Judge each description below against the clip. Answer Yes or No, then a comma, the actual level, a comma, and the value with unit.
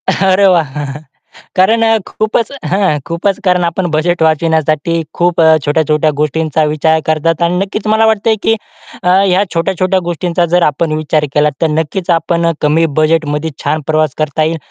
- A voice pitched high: No, medium, 165 Hz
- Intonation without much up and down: No, average, 3.1 semitones